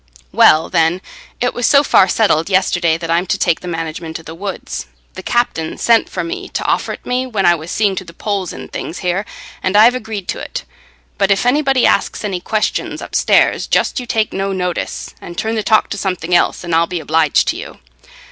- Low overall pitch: No, medium, 185 Hz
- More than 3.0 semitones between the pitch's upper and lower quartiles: Yes, average, 4.6 semitones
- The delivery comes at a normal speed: No, fast, 215 wpm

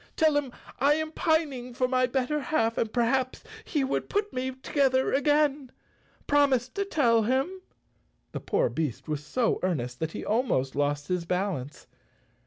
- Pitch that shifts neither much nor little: No, wide, 7.5 semitones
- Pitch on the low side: No, very high, 255 Hz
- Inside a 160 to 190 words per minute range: Yes, average, 165 wpm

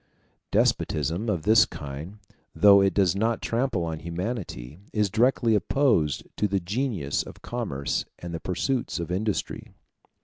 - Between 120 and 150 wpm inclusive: Yes, average, 140 wpm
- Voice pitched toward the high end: No, low, 100 Hz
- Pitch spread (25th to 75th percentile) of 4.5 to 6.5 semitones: Yes, average, 5.3 semitones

